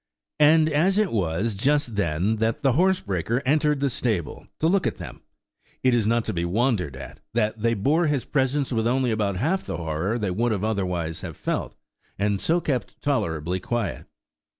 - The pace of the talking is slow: No, average, 180 wpm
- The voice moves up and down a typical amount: No, wide, 6.5 semitones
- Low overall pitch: Yes, low, 115 Hz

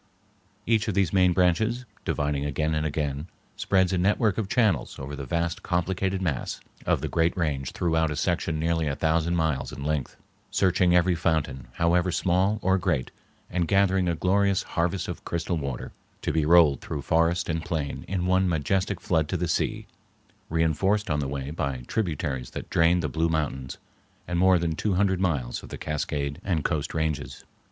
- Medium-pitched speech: No, very low, 85 Hz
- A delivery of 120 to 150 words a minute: No, average, 180 wpm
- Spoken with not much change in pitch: No, average, 3.4 semitones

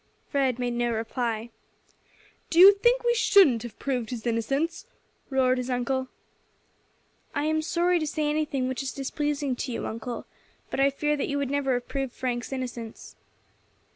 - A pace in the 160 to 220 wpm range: Yes, average, 170 wpm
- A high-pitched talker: Yes, very high, 265 Hz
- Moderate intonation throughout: Yes, average, 3.5 semitones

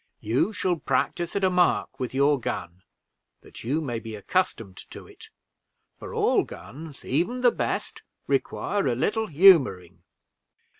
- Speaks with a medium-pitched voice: Yes, medium, 145 Hz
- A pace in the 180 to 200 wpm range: No, average, 145 wpm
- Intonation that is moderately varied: No, wide, 7.3 semitones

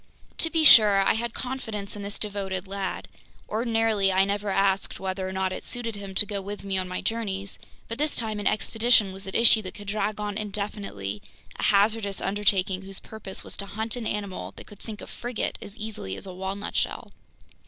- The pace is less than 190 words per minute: No, fast, 205 wpm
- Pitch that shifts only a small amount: Yes, narrow, 2.2 semitones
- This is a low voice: No, high, 205 Hz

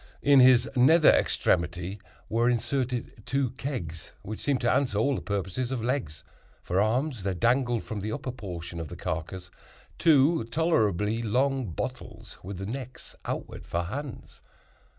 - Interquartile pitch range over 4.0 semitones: Yes, wide, 5.5 semitones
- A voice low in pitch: Yes, low, 115 Hz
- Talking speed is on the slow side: No, average, 150 wpm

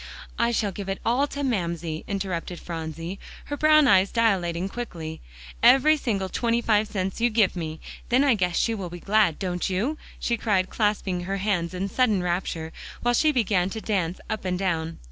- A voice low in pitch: No, high, 195 Hz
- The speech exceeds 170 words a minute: Yes, average, 185 wpm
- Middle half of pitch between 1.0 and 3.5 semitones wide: No, average, 4.6 semitones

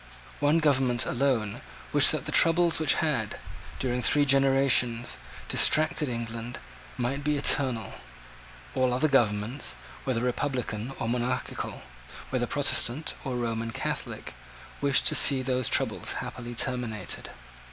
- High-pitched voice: No, low, 125 Hz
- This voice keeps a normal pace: No, slow, 120 wpm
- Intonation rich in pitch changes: No, average, 2.9 semitones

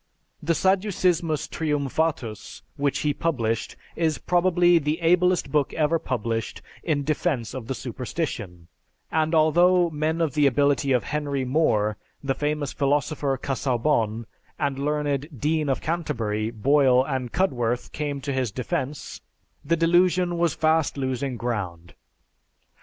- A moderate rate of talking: No, slow, 130 wpm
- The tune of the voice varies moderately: Yes, average, 4.1 semitones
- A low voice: No, medium, 145 Hz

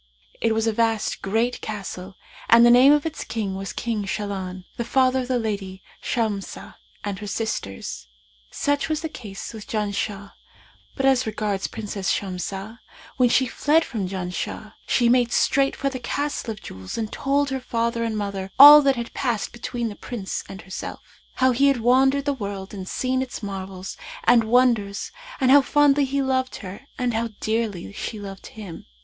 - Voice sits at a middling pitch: No, high, 225 Hz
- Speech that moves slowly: No, average, 180 wpm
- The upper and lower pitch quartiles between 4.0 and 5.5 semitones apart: Yes, average, 4.5 semitones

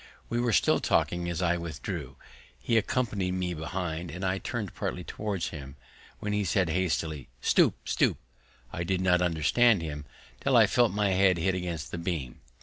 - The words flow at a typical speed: Yes, average, 175 wpm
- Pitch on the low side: Yes, very low, 90 Hz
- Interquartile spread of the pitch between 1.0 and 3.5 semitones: Yes, average, 3.2 semitones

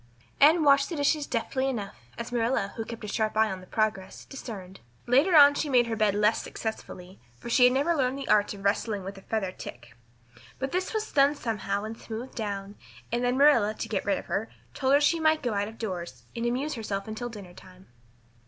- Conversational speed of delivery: No, fast, 220 wpm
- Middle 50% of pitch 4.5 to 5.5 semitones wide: Yes, average, 5.1 semitones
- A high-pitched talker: Yes, high, 225 Hz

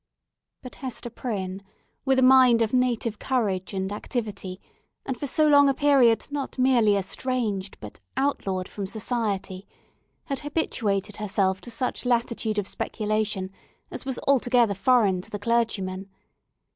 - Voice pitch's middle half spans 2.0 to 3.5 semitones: No, average, 4.4 semitones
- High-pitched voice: Yes, high, 225 Hz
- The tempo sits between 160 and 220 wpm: No, average, 140 wpm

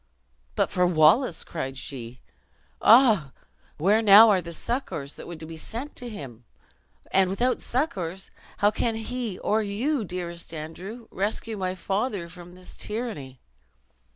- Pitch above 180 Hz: Yes, high, 190 Hz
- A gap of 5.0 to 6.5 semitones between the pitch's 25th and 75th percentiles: Yes, average, 5.3 semitones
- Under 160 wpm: Yes, average, 145 wpm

